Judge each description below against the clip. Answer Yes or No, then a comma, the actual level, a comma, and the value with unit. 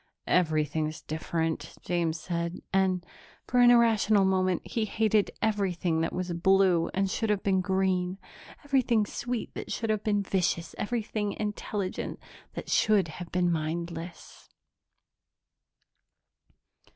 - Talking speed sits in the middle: No, slow, 120 wpm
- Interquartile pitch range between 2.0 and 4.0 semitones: Yes, average, 3.7 semitones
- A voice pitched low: No, high, 190 Hz